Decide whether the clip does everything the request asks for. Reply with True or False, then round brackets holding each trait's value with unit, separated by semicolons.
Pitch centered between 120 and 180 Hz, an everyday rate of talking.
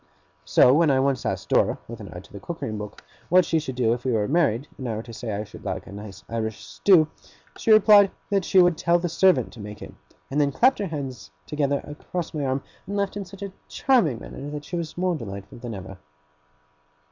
False (140 Hz; 240 wpm)